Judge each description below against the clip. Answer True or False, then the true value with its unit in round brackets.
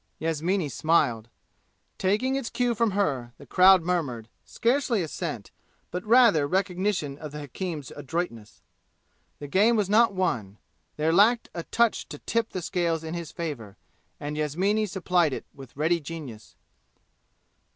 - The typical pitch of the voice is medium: True (170 Hz)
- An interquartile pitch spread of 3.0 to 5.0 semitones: False (5.5 semitones)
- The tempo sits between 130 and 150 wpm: True (140 wpm)